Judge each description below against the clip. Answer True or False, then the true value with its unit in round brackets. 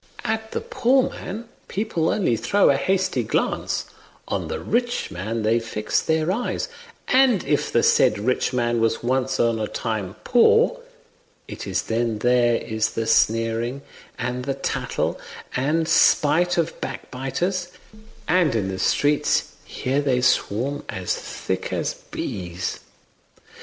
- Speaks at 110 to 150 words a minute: True (140 wpm)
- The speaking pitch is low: True (130 Hz)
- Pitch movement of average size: False (7.8 semitones)